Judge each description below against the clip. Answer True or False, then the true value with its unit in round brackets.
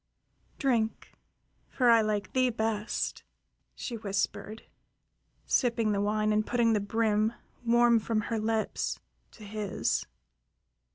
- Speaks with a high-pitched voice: True (220 Hz)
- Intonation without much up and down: True (1.6 semitones)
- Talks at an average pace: False (115 wpm)